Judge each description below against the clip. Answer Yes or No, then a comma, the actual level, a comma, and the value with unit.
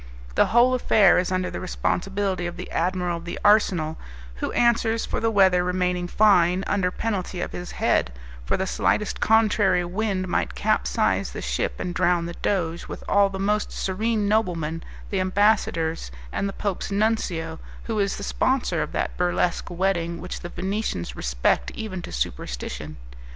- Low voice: No, medium, 185 Hz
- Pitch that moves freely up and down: No, average, 3.1 semitones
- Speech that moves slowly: No, average, 165 wpm